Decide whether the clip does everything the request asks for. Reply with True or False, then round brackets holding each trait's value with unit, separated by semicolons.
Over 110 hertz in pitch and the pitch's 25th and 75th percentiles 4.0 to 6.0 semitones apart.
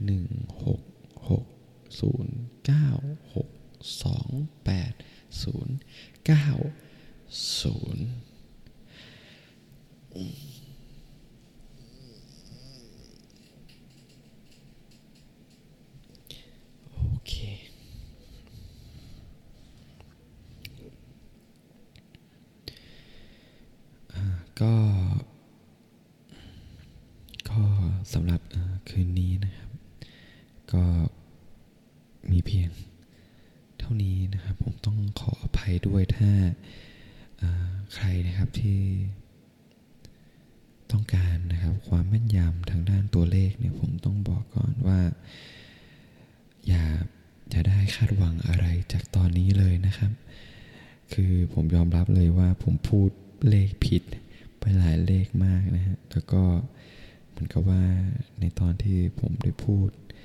False (100 Hz; 4.7 semitones)